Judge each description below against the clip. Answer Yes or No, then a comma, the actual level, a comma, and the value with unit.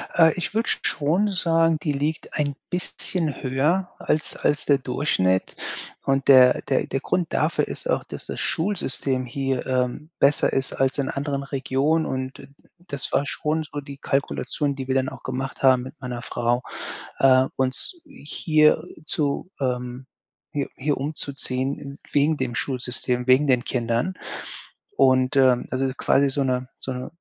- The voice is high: No, low, 135 Hz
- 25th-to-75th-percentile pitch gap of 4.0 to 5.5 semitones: No, average, 2.7 semitones